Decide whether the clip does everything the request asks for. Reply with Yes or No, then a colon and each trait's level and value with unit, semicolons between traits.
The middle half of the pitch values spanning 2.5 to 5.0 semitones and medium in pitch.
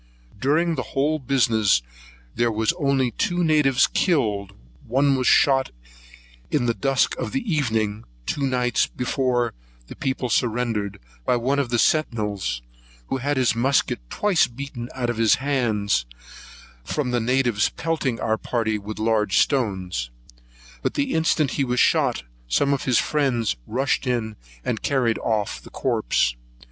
No: average, 4.0 semitones; low, 125 Hz